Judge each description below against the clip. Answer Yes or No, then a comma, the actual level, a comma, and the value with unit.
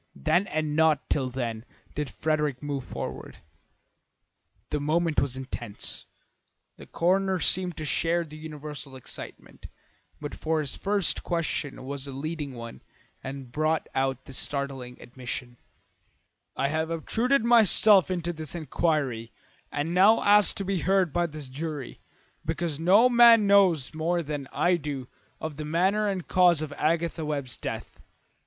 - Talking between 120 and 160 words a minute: Yes, average, 145 wpm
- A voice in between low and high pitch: Yes, medium, 155 Hz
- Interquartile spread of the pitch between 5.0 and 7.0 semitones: No, average, 4.1 semitones